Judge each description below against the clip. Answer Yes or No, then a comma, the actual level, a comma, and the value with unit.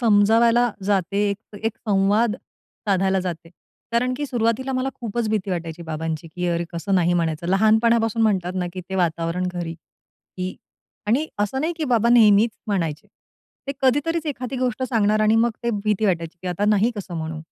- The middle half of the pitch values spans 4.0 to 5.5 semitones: Yes, average, 4.7 semitones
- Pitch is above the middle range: Yes, high, 205 Hz